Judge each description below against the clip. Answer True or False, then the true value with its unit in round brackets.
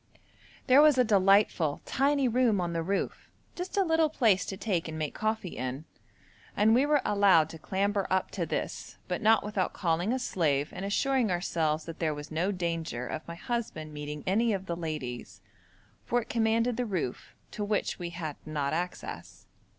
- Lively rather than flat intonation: True (5.8 semitones)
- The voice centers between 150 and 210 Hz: True (190 Hz)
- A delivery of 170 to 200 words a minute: True (185 wpm)